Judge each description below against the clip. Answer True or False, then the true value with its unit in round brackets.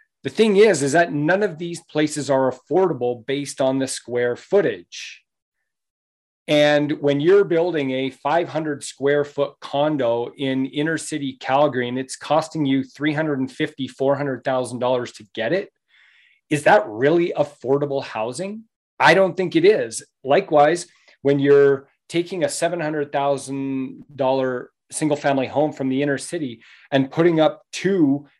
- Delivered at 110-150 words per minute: True (135 wpm)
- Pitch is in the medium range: True (145 Hz)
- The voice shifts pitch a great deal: False (3.5 semitones)